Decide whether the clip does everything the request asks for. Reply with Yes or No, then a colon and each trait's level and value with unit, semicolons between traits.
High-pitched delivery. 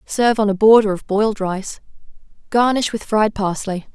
Yes: high, 210 Hz